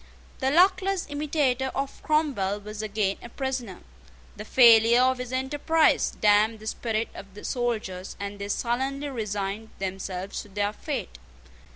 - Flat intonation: No, average, 4.6 semitones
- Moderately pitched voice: No, high, 225 Hz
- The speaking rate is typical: Yes, average, 145 wpm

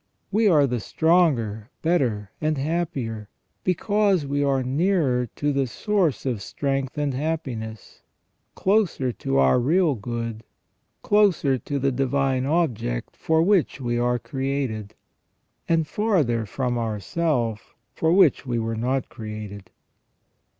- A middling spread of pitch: No, wide, 5.7 semitones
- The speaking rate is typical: No, slow, 125 wpm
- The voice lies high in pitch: No, low, 135 Hz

